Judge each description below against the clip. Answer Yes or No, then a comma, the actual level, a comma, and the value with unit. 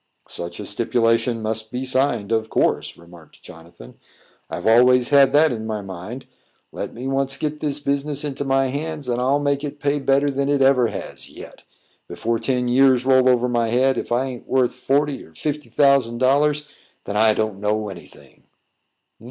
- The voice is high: No, low, 130 Hz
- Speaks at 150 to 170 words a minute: No, average, 185 wpm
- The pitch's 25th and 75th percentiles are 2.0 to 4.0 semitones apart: Yes, average, 3.6 semitones